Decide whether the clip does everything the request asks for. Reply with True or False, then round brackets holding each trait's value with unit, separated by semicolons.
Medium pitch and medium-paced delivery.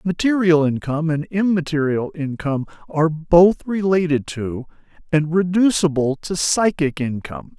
False (160 Hz; 110 wpm)